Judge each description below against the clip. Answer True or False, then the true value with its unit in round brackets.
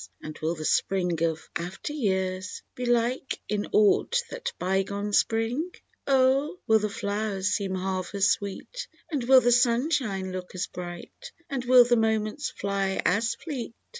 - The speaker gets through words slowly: False (155 wpm)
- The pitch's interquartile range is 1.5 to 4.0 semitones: False (4.8 semitones)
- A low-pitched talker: False (210 Hz)